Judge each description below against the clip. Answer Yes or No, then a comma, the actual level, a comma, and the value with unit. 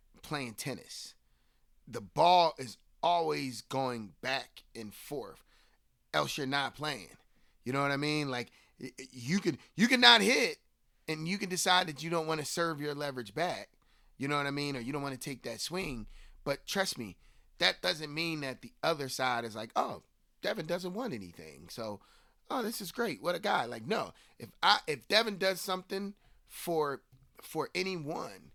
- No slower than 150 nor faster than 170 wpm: No, average, 185 wpm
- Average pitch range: No, wide, 5.9 semitones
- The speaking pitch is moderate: Yes, medium, 150 Hz